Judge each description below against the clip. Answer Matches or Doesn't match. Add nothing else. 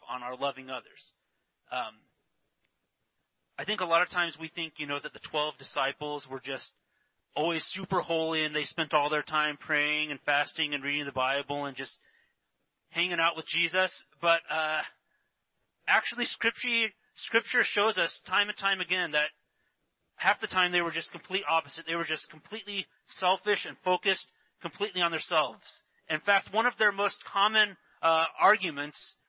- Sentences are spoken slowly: Doesn't match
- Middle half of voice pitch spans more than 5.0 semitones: Doesn't match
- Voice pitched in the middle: Matches